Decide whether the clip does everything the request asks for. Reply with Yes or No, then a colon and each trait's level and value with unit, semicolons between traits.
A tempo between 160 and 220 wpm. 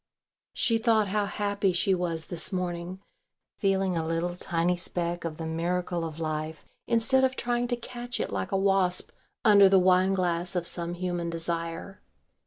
Yes: average, 170 wpm